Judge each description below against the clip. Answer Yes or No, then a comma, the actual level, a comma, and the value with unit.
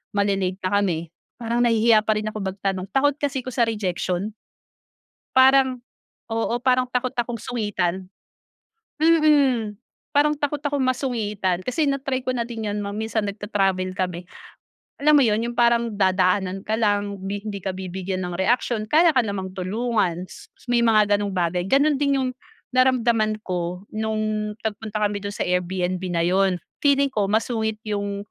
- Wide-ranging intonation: No, average, 4.2 semitones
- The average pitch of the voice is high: Yes, high, 215 Hz